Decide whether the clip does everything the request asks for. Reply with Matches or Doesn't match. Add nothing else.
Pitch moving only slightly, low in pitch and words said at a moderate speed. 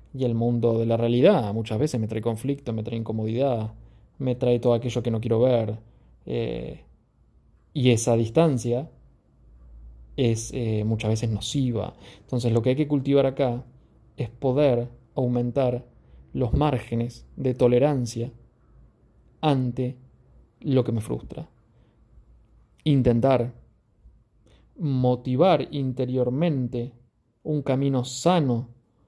Doesn't match